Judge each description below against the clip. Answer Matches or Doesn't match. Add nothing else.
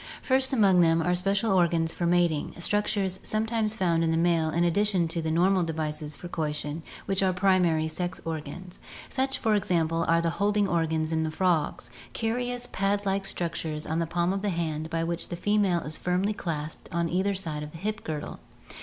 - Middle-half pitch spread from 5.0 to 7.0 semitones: Doesn't match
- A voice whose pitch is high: Doesn't match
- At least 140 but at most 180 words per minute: Doesn't match